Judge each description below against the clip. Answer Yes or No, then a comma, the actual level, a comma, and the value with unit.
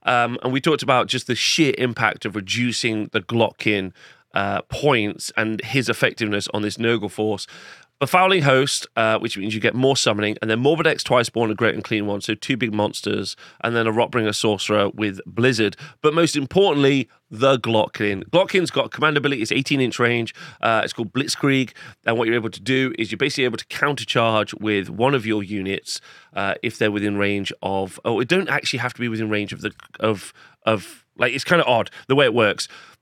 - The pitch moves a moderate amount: Yes, average, 3.7 semitones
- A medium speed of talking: No, fast, 215 wpm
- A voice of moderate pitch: No, low, 115 Hz